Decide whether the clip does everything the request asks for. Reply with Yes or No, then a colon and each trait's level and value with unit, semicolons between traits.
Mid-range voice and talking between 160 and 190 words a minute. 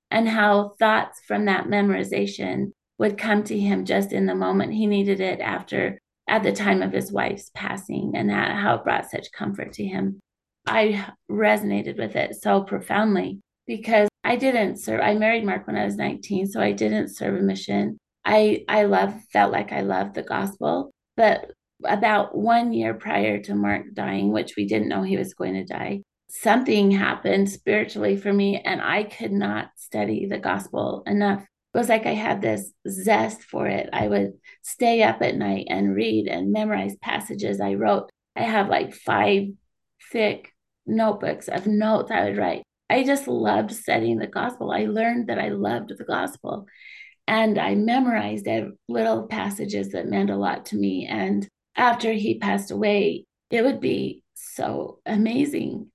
No: high, 195 Hz; average, 175 wpm